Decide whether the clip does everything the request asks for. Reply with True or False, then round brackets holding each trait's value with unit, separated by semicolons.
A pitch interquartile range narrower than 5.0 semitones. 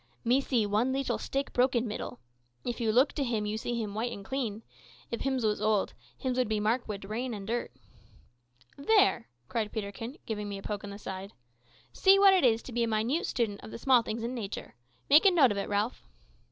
True (3.5 semitones)